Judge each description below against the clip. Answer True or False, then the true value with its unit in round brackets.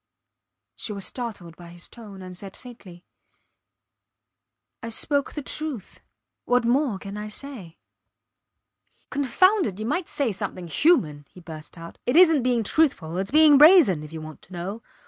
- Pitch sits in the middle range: False (215 Hz)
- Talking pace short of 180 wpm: True (160 wpm)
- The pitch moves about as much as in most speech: False (7.9 semitones)